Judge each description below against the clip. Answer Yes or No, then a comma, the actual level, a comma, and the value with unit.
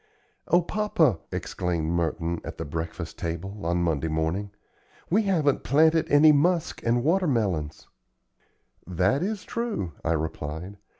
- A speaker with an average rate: No, slow, 130 wpm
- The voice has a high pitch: No, low, 100 Hz